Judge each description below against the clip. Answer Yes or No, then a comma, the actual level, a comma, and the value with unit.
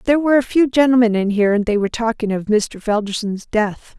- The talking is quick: Yes, fast, 225 wpm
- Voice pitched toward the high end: Yes, high, 225 Hz